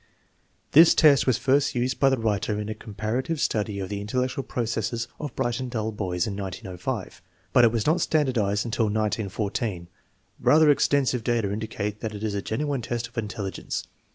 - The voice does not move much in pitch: No, average, 3.7 semitones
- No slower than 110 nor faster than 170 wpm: No, average, 180 wpm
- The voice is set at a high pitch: No, low, 110 Hz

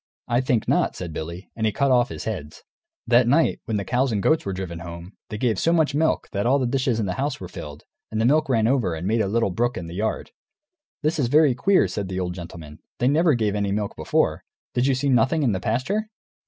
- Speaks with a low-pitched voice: Yes, low, 115 Hz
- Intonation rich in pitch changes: Yes, wide, 5.9 semitones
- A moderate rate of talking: No, fast, 255 wpm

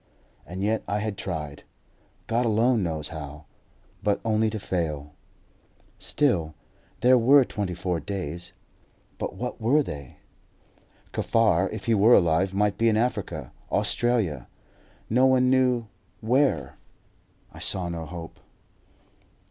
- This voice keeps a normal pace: No, slow, 125 wpm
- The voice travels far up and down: Yes, wide, 6.0 semitones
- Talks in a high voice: No, low, 100 Hz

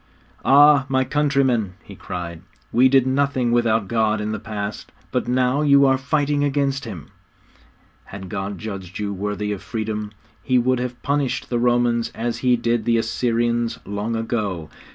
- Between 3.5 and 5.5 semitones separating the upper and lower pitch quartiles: Yes, average, 3.8 semitones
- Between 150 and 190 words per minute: Yes, average, 160 wpm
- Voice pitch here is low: Yes, low, 120 Hz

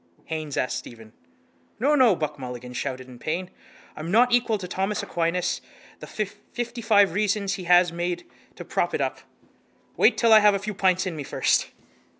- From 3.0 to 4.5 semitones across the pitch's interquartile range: No, wide, 5.4 semitones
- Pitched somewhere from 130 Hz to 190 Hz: Yes, medium, 185 Hz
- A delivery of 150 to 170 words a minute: No, average, 185 wpm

